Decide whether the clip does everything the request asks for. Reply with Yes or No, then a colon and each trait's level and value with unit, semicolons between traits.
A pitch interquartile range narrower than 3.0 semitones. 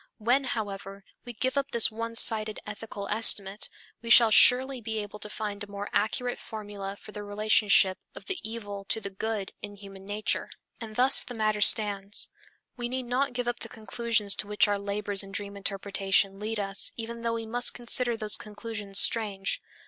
Yes: narrow, 2.4 semitones